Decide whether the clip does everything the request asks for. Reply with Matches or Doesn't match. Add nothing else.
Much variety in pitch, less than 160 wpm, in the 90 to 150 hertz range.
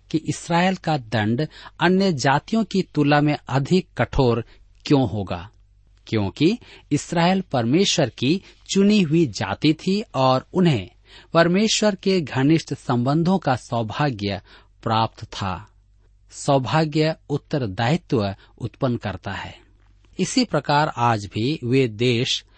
Matches